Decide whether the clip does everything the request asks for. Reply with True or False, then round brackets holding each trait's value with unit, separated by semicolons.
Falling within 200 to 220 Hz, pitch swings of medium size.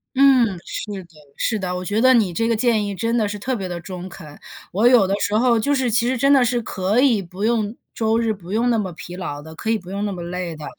True (210 Hz; 4.3 semitones)